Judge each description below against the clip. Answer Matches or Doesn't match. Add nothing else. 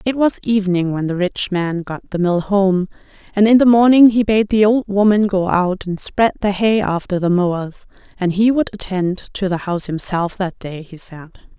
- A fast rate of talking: Matches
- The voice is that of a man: Doesn't match